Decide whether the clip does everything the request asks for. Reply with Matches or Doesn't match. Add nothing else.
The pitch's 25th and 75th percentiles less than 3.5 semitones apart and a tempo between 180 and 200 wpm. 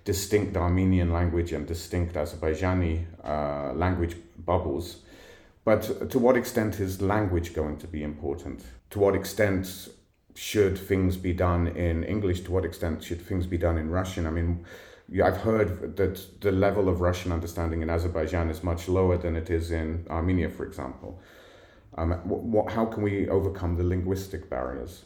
Doesn't match